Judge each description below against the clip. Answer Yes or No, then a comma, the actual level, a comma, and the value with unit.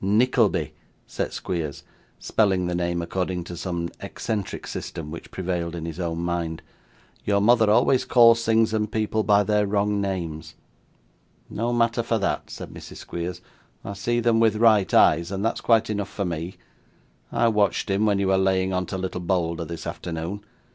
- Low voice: Yes, very low, 95 Hz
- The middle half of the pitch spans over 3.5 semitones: Yes, average, 3.9 semitones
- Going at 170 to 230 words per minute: Yes, average, 175 wpm